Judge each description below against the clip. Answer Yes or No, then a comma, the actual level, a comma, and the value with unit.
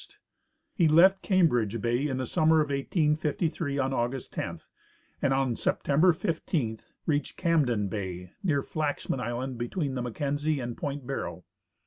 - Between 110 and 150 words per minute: Yes, average, 140 wpm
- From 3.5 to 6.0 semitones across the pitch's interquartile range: Yes, average, 4.5 semitones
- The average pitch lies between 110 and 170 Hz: Yes, medium, 140 Hz